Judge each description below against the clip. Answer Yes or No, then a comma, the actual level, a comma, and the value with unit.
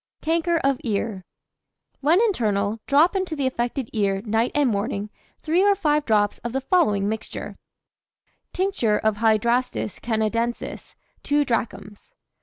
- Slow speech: Yes, slow, 130 wpm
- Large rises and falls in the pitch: Yes, wide, 5.8 semitones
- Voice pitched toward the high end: Yes, high, 240 Hz